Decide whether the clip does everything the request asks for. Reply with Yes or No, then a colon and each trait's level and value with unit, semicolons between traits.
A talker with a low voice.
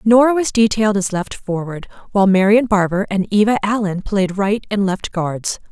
No: high, 205 Hz